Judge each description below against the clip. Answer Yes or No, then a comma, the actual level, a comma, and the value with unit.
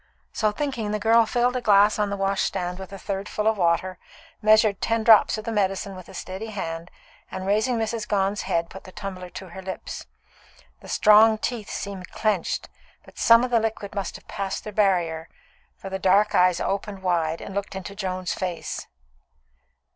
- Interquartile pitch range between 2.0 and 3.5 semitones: Yes, narrow, 2.4 semitones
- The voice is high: Yes, high, 200 Hz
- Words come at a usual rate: Yes, average, 190 wpm